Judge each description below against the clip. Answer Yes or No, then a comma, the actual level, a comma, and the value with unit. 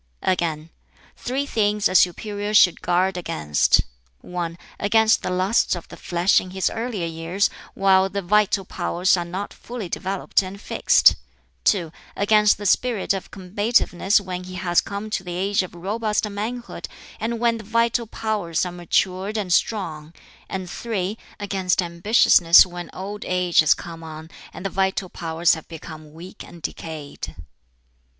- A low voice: No, high, 190 Hz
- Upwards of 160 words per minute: No, average, 155 wpm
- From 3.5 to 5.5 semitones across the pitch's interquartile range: No, average, 3.1 semitones